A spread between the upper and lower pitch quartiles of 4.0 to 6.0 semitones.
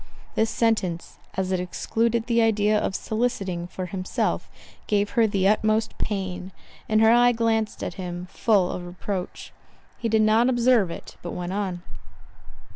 No: average, 3.5 semitones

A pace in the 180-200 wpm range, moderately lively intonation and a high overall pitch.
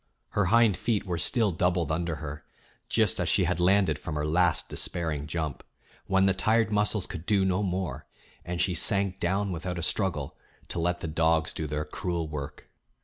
No: average, 190 wpm; average, 3.4 semitones; very low, 90 Hz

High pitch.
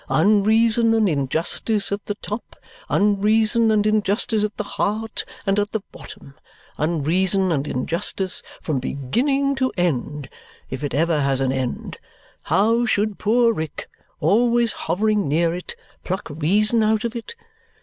Yes: high, 205 Hz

